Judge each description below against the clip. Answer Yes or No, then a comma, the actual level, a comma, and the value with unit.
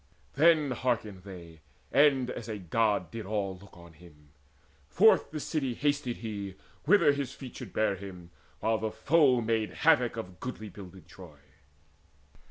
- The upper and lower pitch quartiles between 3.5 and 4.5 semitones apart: No, wide, 5.6 semitones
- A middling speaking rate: Yes, average, 160 wpm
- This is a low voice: Yes, low, 110 Hz